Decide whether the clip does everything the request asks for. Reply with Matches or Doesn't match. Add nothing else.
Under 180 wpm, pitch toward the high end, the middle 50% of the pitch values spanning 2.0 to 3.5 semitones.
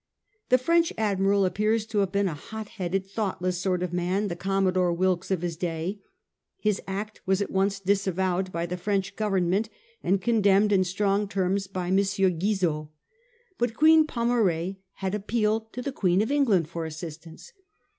Matches